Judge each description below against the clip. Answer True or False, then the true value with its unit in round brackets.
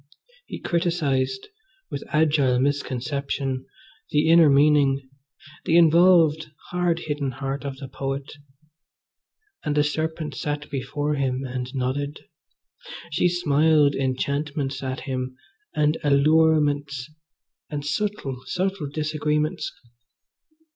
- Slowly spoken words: True (100 wpm)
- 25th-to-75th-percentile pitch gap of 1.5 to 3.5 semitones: True (2.6 semitones)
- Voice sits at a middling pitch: True (145 Hz)